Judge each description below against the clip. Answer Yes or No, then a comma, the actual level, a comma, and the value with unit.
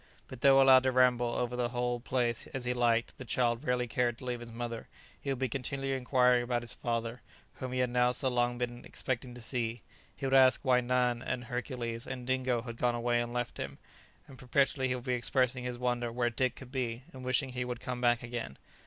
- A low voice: Yes, low, 125 Hz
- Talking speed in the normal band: No, fast, 230 wpm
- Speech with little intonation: Yes, narrow, 1.2 semitones